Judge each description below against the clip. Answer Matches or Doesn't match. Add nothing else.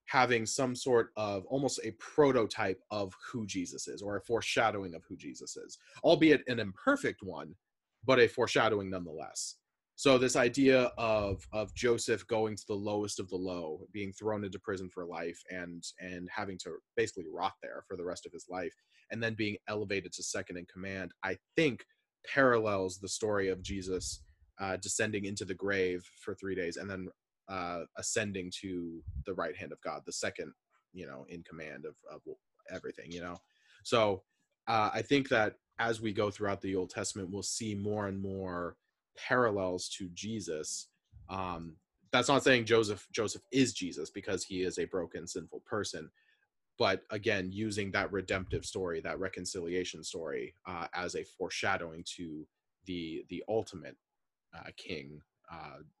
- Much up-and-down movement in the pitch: Doesn't match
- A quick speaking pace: Doesn't match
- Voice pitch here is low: Matches